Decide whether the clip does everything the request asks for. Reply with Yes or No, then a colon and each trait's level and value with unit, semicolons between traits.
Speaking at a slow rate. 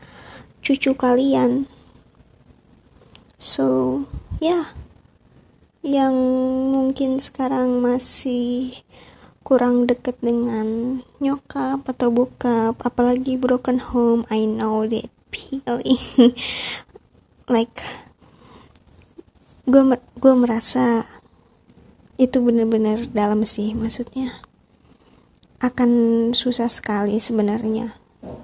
Yes: slow, 75 wpm